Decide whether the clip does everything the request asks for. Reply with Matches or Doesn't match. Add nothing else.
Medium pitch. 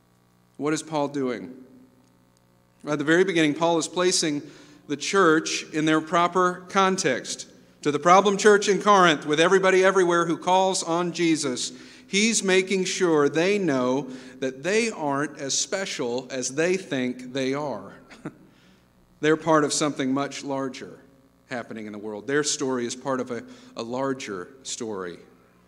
Matches